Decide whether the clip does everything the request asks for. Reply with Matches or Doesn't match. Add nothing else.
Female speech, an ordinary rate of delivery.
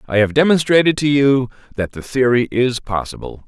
Doesn't match